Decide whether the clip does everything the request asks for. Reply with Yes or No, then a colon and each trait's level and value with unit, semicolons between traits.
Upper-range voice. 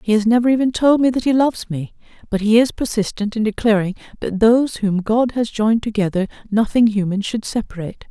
Yes: high, 220 Hz